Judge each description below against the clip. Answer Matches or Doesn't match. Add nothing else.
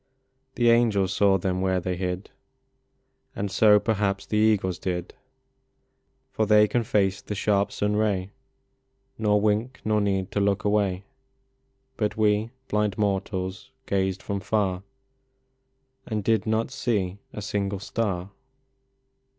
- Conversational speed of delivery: Doesn't match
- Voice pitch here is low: Matches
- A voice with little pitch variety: Matches